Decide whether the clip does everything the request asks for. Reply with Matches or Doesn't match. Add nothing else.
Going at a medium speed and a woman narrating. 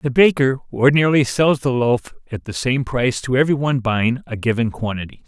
Doesn't match